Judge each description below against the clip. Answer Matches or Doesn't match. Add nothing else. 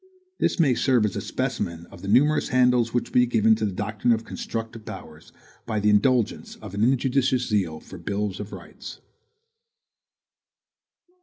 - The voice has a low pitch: Matches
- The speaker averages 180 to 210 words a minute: Doesn't match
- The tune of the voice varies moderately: Matches